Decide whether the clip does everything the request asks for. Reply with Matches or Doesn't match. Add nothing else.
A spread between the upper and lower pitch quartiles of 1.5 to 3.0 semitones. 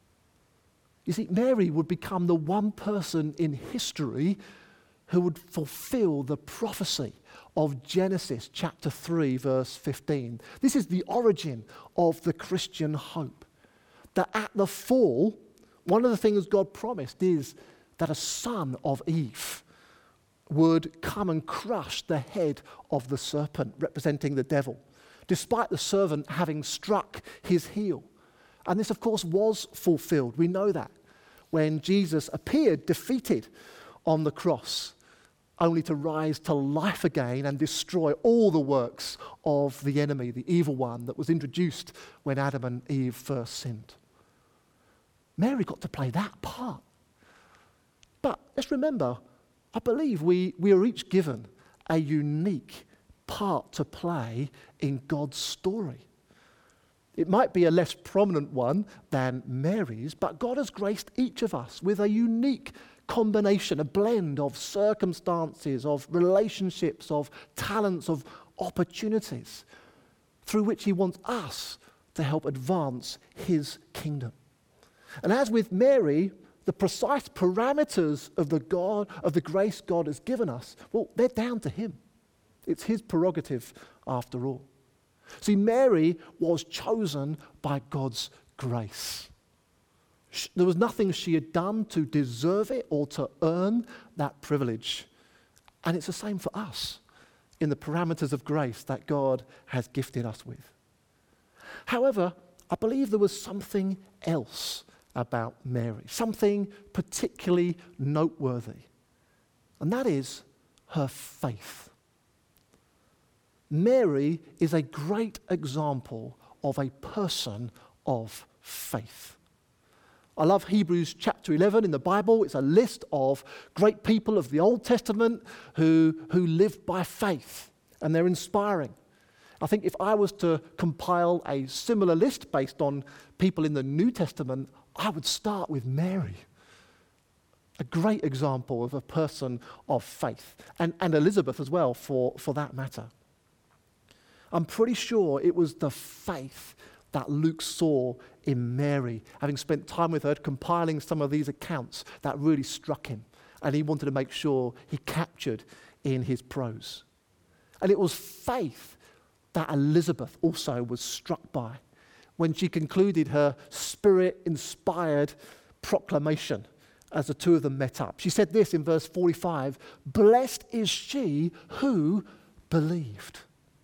Doesn't match